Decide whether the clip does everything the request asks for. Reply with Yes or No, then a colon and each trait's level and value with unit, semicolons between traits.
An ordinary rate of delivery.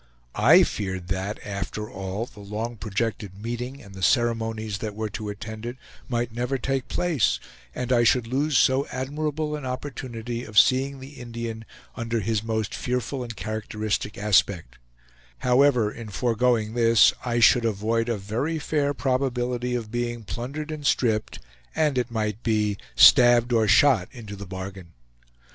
Yes: average, 155 wpm